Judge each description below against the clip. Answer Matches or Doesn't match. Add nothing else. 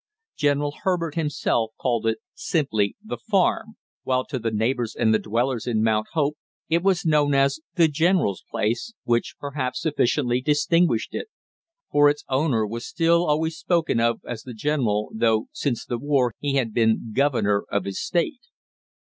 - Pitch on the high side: Doesn't match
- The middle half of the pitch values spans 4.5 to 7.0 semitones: Matches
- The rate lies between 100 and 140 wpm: Doesn't match